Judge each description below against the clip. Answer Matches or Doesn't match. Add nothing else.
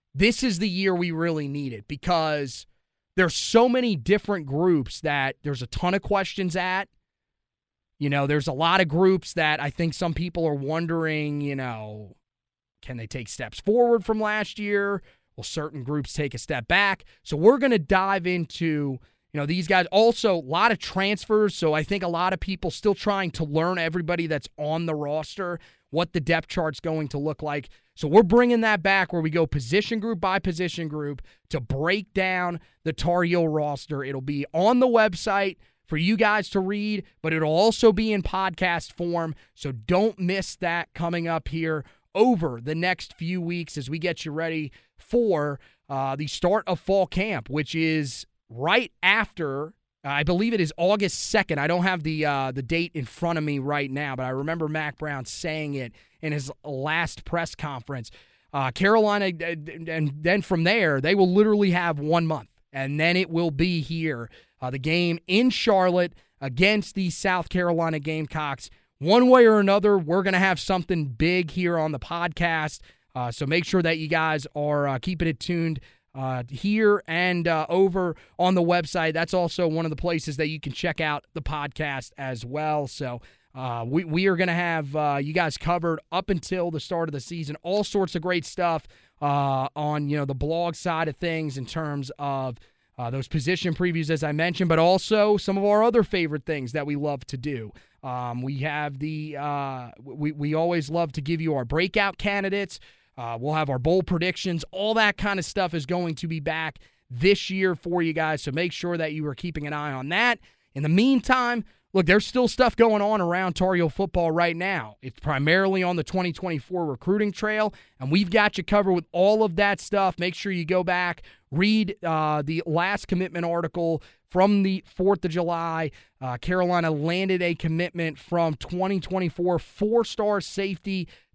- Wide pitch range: Doesn't match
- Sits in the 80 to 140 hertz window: Doesn't match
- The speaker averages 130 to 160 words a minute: Doesn't match